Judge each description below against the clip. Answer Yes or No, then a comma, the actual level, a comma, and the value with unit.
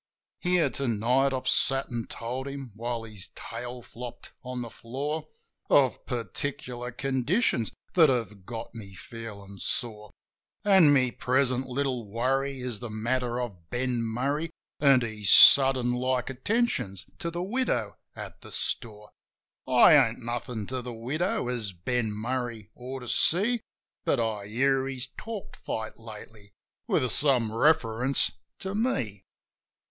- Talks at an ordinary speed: Yes, average, 145 wpm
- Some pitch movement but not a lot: Yes, average, 3.1 semitones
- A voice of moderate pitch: No, low, 125 Hz